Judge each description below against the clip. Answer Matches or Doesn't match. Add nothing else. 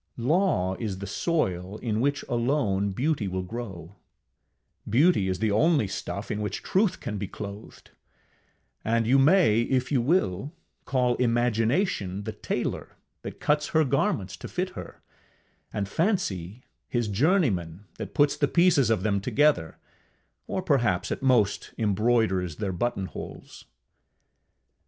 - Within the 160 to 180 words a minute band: Doesn't match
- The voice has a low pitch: Matches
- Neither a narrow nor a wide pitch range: Doesn't match